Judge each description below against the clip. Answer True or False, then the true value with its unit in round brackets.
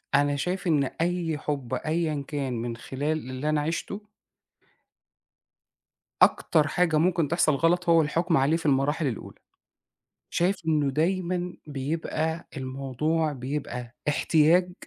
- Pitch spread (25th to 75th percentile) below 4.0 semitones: True (3.3 semitones)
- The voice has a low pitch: False (155 Hz)